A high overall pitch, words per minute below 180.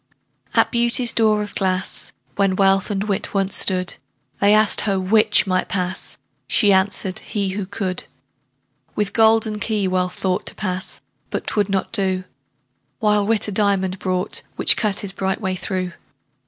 Yes: high, 195 Hz; average, 160 wpm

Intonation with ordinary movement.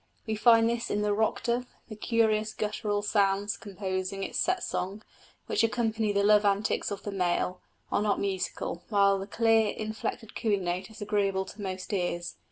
No: narrow, 2.1 semitones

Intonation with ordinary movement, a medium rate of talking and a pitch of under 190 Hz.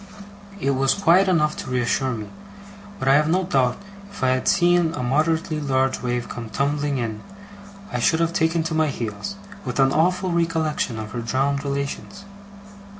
Yes: average, 4.4 semitones; average, 175 wpm; medium, 140 Hz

